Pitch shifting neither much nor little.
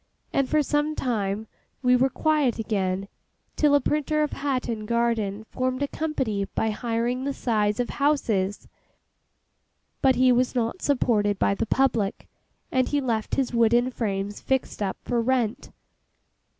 Yes: average, 3.9 semitones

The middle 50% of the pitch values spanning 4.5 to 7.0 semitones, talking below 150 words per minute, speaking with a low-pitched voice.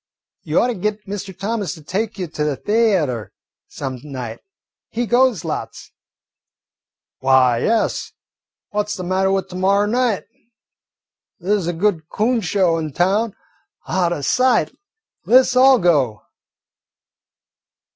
No: wide, 5.4 semitones; average, 140 wpm; high, 190 Hz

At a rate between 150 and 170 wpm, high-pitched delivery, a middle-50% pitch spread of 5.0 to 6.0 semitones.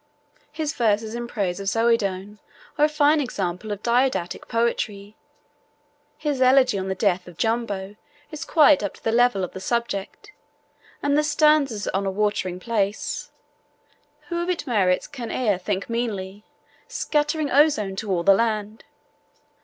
Yes: average, 155 wpm; high, 225 Hz; wide, 5.4 semitones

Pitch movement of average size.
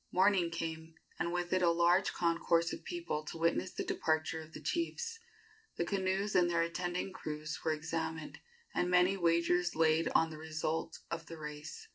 No: narrow, 2.1 semitones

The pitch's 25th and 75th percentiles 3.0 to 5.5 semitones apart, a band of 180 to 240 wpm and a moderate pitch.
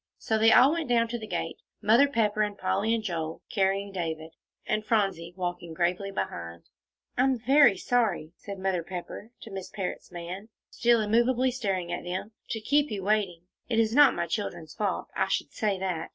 No: average, 4.3 semitones; average, 190 wpm; high, 200 Hz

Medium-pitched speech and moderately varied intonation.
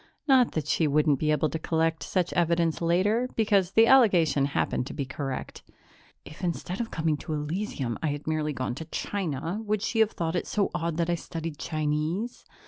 Yes: medium, 165 Hz; average, 4.1 semitones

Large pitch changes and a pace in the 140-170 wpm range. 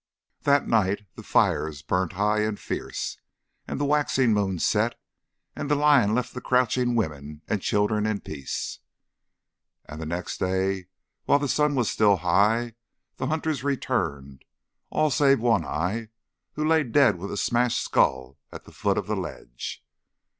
Yes: wide, 6.2 semitones; average, 160 wpm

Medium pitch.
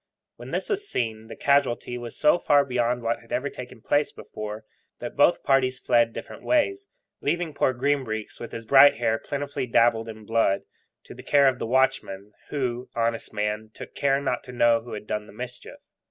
No: low, 120 Hz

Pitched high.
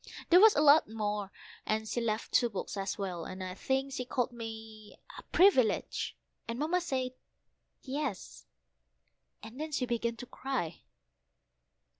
Yes: high, 235 Hz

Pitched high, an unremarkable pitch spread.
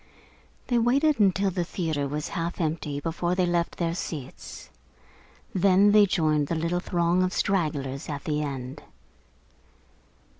No: medium, 170 Hz; average, 3.8 semitones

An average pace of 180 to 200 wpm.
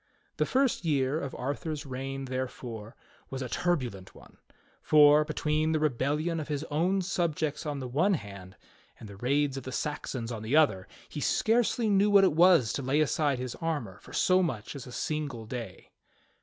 Yes: average, 185 wpm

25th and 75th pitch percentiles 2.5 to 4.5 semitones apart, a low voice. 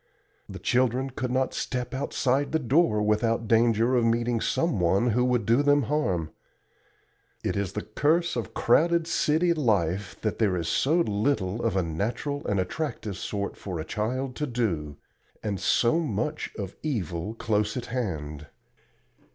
No: average, 5.1 semitones; low, 115 Hz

